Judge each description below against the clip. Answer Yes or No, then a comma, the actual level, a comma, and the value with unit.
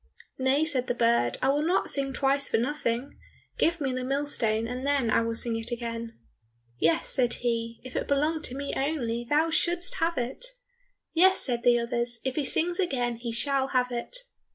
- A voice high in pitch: Yes, very high, 255 Hz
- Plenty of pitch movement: No, average, 3.5 semitones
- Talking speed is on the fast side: No, average, 195 wpm